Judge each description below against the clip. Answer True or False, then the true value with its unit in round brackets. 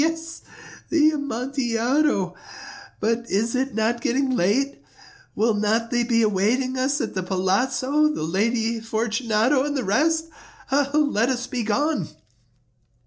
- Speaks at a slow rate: True (130 wpm)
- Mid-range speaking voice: False (240 Hz)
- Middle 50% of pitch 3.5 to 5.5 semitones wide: True (4.1 semitones)